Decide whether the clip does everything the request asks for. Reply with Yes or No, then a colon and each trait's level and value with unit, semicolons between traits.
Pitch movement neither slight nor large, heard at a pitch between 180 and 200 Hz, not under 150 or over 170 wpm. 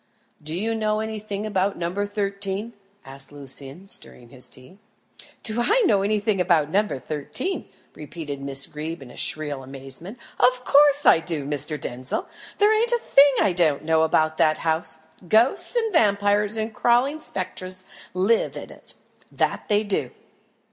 No: wide, 6.2 semitones; high, 190 Hz; average, 155 wpm